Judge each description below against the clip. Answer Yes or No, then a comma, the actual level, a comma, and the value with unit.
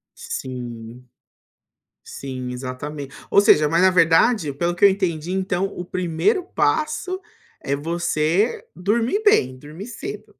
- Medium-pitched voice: Yes, medium, 170 Hz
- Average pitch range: No, wide, 6.2 semitones